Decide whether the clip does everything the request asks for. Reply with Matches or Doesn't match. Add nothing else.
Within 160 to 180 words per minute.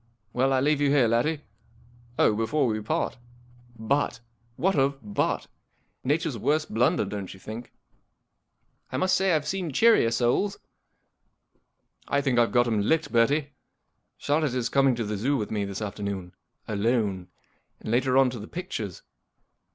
Matches